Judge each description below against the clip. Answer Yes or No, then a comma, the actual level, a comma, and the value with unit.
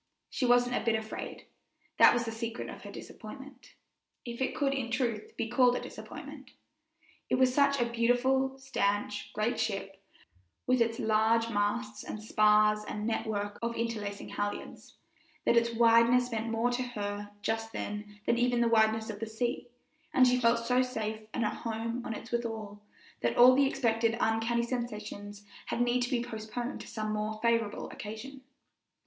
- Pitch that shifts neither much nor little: No, narrow, 2.2 semitones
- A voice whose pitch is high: Yes, high, 230 Hz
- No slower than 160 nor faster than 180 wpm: Yes, average, 170 wpm